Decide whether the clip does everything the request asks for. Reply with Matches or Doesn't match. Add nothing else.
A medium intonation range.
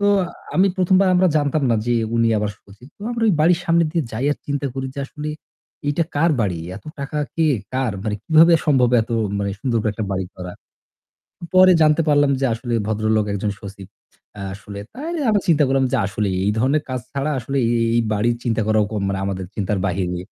Doesn't match